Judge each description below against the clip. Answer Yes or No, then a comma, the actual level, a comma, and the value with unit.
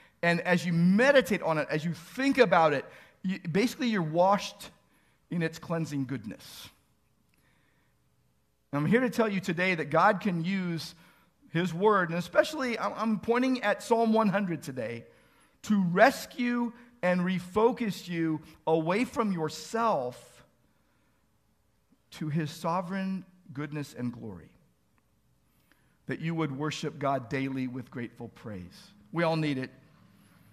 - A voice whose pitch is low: No, medium, 175 Hz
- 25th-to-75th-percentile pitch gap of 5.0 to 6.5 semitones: Yes, wide, 5.4 semitones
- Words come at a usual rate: No, slow, 130 wpm